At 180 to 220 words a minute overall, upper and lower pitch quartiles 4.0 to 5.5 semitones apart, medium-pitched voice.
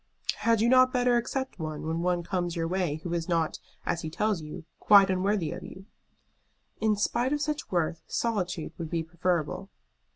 Yes: average, 185 wpm; average, 4.9 semitones; medium, 180 Hz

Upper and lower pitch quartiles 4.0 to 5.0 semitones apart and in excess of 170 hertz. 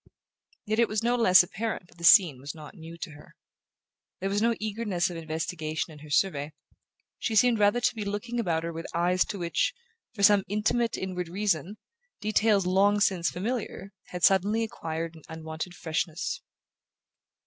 Yes: average, 4.3 semitones; medium, 185 Hz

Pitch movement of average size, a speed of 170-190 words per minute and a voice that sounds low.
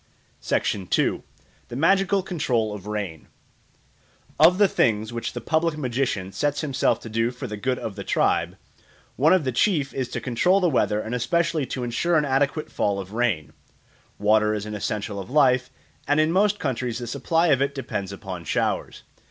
No: wide, 6.3 semitones; average, 180 wpm; low, 125 Hz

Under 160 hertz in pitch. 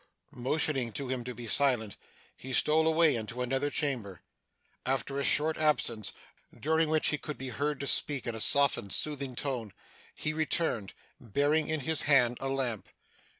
Yes: low, 135 Hz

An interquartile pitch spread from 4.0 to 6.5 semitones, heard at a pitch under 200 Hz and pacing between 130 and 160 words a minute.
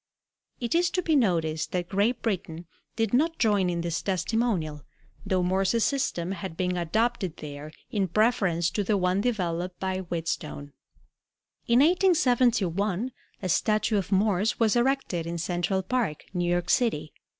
Yes: average, 5.0 semitones; high, 190 Hz; average, 150 wpm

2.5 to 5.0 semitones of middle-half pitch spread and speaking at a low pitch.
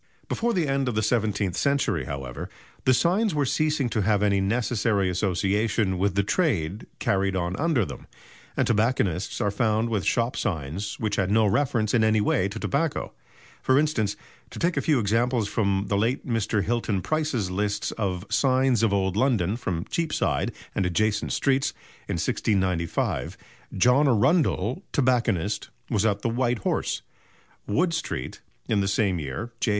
Yes: average, 4.6 semitones; low, 110 Hz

